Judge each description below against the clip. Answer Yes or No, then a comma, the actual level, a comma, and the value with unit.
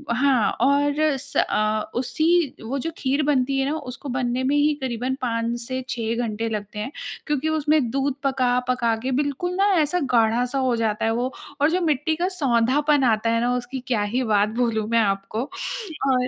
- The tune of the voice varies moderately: Yes, average, 3.6 semitones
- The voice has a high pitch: Yes, very high, 255 Hz